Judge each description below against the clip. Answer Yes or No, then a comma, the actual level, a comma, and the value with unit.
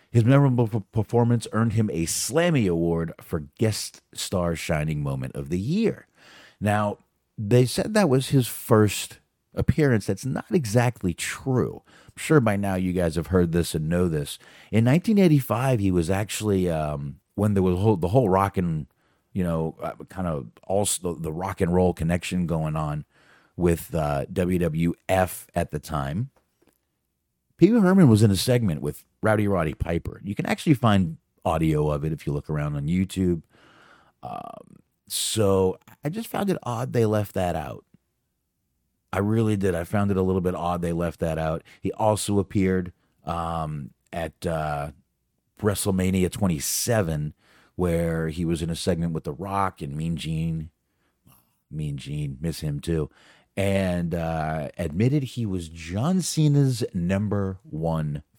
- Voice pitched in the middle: No, very low, 95 Hz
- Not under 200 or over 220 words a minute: No, average, 160 wpm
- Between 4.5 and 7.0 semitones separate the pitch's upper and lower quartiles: Yes, average, 5.1 semitones